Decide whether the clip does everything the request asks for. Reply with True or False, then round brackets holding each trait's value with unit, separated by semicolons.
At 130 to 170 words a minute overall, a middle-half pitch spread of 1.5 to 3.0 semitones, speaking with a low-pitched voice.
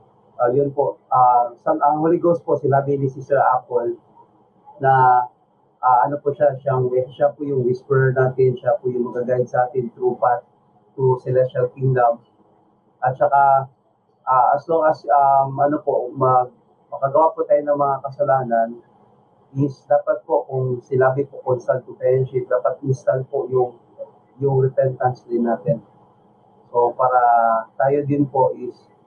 True (155 wpm; 2.5 semitones; 130 Hz)